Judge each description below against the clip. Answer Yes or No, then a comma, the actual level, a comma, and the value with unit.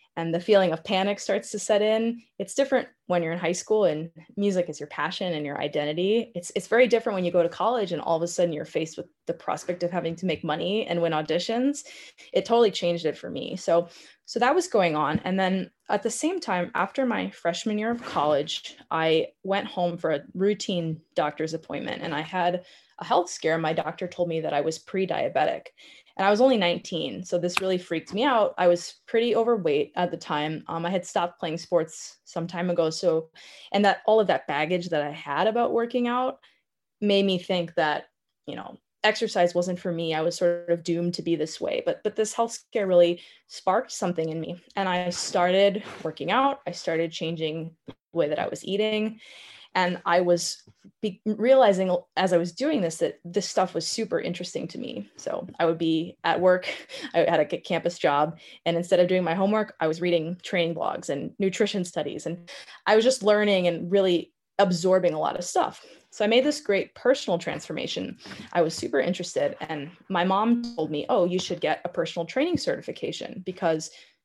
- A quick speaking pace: Yes, fast, 210 wpm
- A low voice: No, medium, 180 Hz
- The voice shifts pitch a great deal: No, average, 4.1 semitones